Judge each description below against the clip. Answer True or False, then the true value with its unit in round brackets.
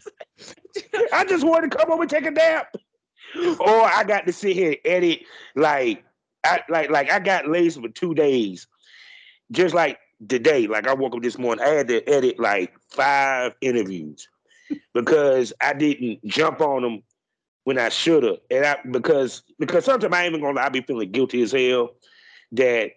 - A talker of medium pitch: True (175 Hz)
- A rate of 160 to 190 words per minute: True (180 wpm)